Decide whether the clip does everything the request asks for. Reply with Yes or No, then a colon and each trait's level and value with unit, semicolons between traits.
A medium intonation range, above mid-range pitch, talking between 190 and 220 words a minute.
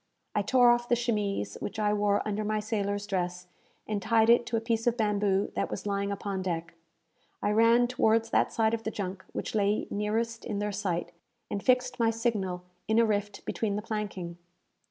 No: narrow, 2.3 semitones; high, 210 Hz; average, 195 wpm